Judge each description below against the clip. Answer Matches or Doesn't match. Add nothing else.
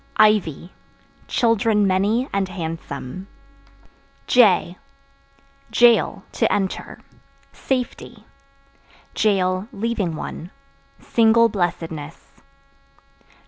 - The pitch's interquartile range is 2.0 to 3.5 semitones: Doesn't match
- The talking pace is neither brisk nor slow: Doesn't match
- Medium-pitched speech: Doesn't match